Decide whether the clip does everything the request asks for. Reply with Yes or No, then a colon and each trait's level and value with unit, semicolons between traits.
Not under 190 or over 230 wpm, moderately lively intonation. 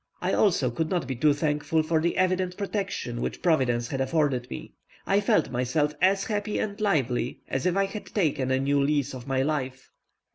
No: average, 195 wpm; wide, 5.8 semitones